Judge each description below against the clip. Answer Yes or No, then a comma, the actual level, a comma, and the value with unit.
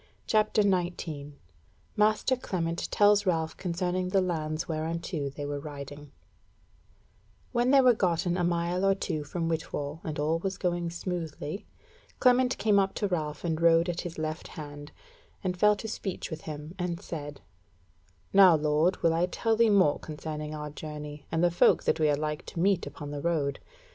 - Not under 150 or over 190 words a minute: Yes, average, 175 wpm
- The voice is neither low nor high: Yes, medium, 170 Hz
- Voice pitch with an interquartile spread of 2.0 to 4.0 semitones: Yes, average, 3.6 semitones